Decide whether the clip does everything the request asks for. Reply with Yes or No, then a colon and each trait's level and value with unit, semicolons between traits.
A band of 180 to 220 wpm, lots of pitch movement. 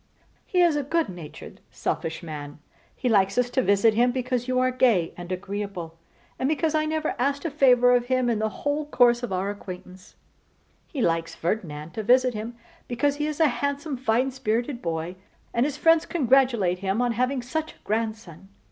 Yes: average, 190 wpm; wide, 5.7 semitones